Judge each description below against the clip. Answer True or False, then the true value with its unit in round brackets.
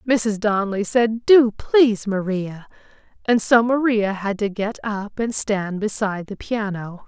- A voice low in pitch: False (215 Hz)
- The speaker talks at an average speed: True (155 wpm)